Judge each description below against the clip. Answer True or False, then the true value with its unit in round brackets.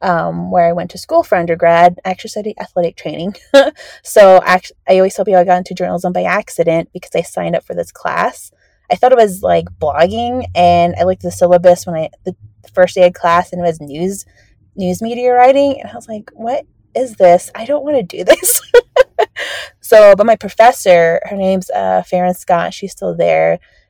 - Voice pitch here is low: False (185 Hz)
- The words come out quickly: True (210 wpm)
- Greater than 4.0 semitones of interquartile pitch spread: True (4.5 semitones)